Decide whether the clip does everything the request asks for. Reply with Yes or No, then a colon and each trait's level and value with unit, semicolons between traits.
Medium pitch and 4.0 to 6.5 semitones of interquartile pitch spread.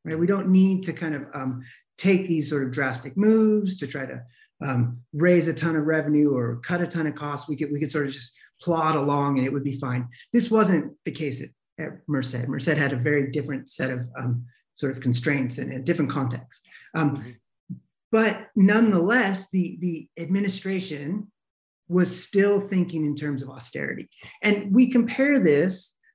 Yes: medium, 155 Hz; wide, 5.6 semitones